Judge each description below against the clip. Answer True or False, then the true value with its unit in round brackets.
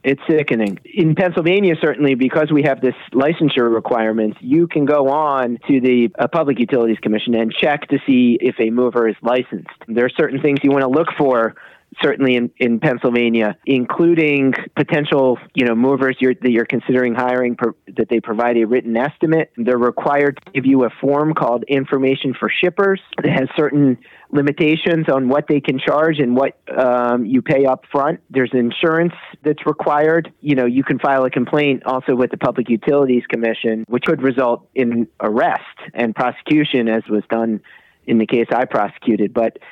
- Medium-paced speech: True (180 wpm)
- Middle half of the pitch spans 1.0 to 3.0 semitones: False (3.7 semitones)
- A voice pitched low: True (130 Hz)